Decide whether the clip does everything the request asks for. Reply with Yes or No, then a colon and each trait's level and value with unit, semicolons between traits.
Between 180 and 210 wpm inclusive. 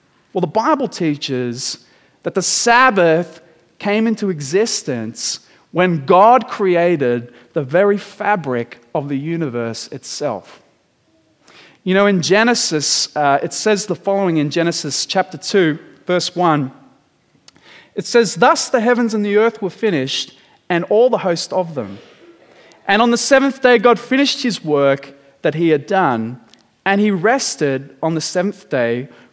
No: average, 145 wpm